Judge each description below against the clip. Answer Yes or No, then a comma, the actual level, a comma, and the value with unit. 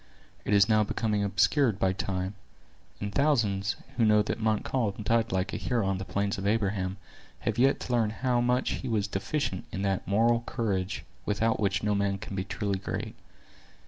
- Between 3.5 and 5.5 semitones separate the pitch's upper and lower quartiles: No, average, 2.8 semitones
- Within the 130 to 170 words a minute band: No, average, 185 wpm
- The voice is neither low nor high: No, low, 105 Hz